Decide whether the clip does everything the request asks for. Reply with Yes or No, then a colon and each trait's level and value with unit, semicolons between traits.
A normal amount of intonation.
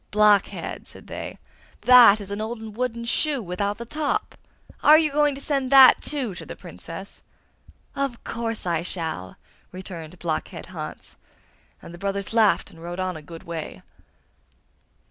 No: wide, 6.0 semitones